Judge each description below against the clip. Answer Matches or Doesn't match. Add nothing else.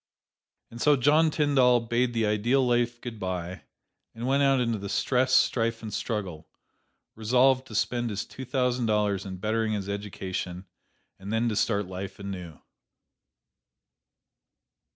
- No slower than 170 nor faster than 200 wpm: Doesn't match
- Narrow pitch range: Doesn't match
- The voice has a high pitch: Doesn't match